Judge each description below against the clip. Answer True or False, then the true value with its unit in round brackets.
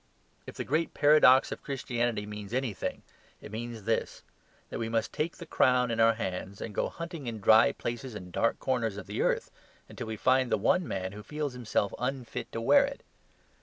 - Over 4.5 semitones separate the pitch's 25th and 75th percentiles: False (3.5 semitones)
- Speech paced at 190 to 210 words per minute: True (200 wpm)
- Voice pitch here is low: True (120 Hz)